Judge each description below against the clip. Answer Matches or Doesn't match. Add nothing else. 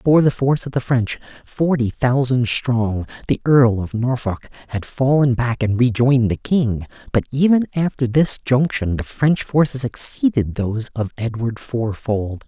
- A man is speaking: Matches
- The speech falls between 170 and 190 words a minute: Doesn't match